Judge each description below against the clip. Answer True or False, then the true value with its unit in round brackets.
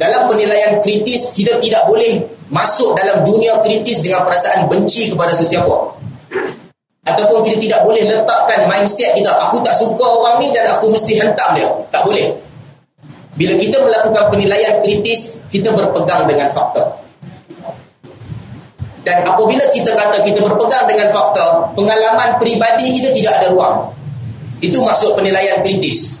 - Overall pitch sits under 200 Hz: False (210 Hz)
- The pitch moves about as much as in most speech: True (3.6 semitones)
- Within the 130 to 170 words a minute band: True (140 wpm)